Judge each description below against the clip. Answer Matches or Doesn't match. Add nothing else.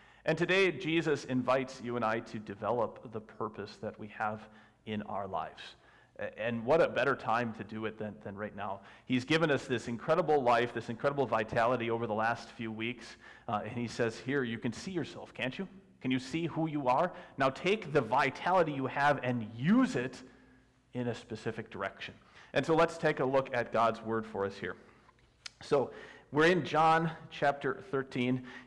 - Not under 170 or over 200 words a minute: Matches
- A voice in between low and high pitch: Doesn't match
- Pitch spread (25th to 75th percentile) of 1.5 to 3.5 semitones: Doesn't match